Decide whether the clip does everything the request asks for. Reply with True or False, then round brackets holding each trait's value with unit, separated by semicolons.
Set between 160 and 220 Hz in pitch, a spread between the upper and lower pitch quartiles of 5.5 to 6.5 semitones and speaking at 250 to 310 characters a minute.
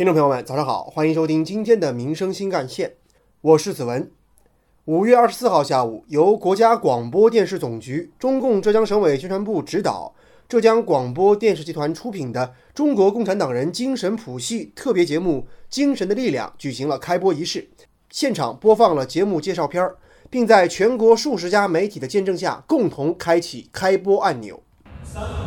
False (185 Hz; 6.9 semitones; 285 characters per minute)